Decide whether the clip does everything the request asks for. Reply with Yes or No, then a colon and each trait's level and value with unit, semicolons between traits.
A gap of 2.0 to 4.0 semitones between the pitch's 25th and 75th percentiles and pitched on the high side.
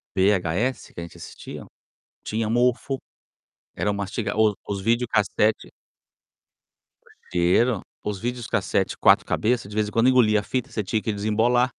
No: average, 3.0 semitones; low, 110 Hz